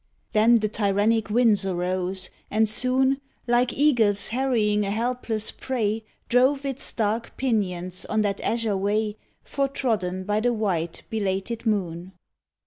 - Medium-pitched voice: No, high, 215 Hz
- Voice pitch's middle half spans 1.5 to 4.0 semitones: Yes, average, 3.3 semitones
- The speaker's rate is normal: No, slow, 130 wpm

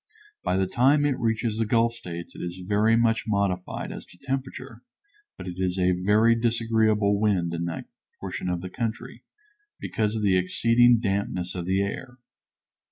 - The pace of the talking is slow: No, average, 170 wpm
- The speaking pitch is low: Yes, low, 105 Hz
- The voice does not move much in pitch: No, average, 4.0 semitones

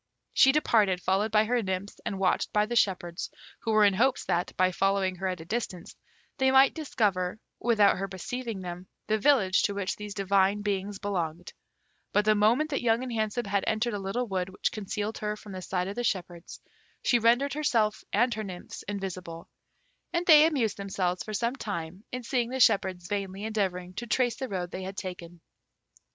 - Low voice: No, high, 205 Hz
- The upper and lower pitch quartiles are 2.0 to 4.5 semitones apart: Yes, average, 3.7 semitones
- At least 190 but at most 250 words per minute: Yes, average, 195 wpm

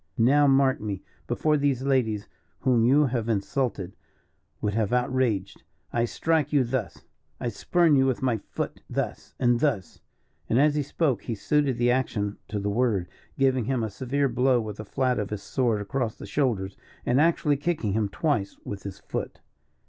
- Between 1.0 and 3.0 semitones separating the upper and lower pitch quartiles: No, average, 4.3 semitones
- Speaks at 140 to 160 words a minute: No, average, 180 wpm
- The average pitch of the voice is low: Yes, low, 125 Hz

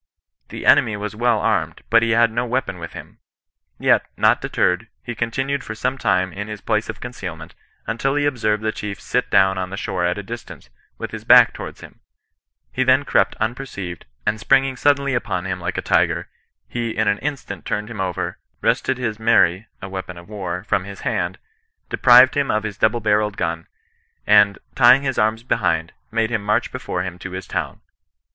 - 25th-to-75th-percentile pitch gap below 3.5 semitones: No, average, 4.0 semitones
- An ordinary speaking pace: Yes, average, 195 wpm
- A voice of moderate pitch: No, low, 110 Hz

